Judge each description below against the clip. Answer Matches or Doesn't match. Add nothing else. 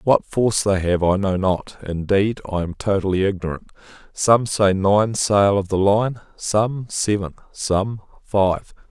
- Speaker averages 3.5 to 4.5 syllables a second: Matches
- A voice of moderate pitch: Doesn't match